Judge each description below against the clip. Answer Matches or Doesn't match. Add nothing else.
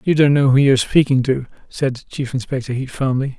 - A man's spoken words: Matches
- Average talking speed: Doesn't match